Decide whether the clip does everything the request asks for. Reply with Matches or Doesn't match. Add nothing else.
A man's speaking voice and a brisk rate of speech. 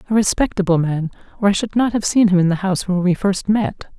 Doesn't match